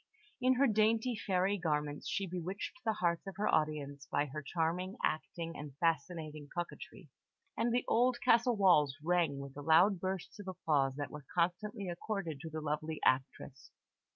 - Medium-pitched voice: Yes, medium, 170 Hz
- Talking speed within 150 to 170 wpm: Yes, average, 165 wpm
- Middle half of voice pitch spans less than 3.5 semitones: No, average, 4.9 semitones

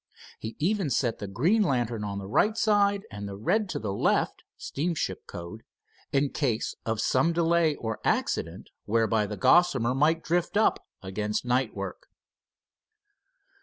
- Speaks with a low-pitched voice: Yes, low, 125 Hz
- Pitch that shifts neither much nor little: No, wide, 8.1 semitones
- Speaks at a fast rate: No, average, 150 wpm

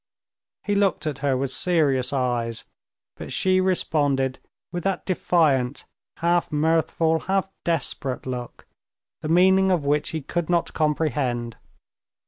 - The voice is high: No, medium, 155 Hz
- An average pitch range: Yes, average, 4.8 semitones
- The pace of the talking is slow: Yes, slow, 125 wpm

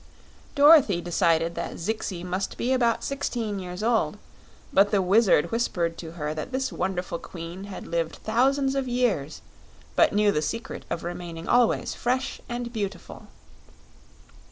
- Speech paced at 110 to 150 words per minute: Yes, average, 145 wpm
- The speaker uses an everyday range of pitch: No, wide, 5.8 semitones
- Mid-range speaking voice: No, high, 200 Hz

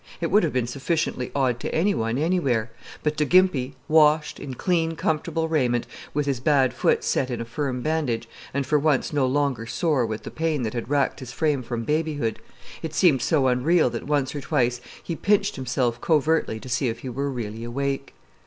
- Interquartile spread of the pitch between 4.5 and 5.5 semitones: No, average, 4.0 semitones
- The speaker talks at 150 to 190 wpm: No, average, 200 wpm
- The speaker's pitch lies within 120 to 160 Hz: Yes, medium, 140 Hz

